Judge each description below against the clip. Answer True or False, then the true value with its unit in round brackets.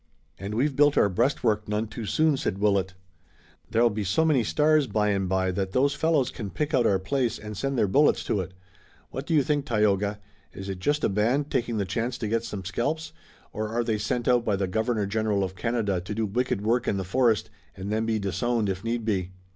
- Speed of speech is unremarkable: False (225 wpm)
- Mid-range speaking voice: False (110 Hz)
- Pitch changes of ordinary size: True (4.0 semitones)